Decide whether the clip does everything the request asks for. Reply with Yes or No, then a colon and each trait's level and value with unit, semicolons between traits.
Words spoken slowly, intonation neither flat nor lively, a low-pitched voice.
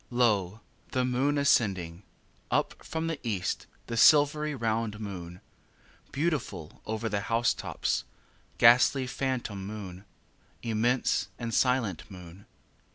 Yes: slow, 115 wpm; average, 4.6 semitones; low, 115 Hz